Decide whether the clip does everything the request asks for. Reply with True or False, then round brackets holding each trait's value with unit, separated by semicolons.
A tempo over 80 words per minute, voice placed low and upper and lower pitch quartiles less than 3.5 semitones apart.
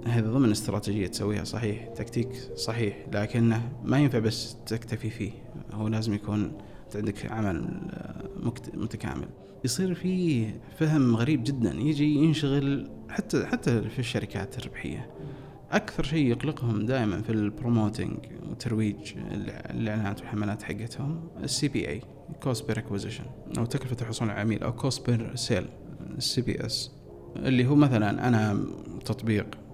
False (130 wpm; 115 Hz; 3.9 semitones)